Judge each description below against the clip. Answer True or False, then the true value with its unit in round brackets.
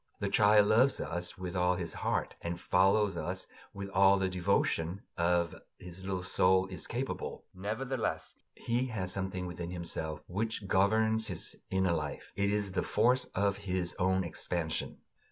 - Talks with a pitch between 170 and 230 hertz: False (95 Hz)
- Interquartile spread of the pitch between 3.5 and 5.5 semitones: False (2.4 semitones)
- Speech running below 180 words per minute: True (160 wpm)